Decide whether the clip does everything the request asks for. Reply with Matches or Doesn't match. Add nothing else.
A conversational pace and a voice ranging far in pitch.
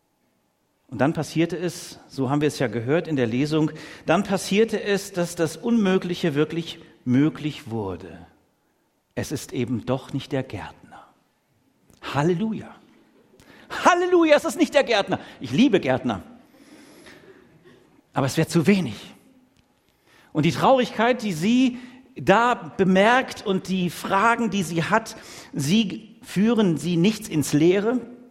Matches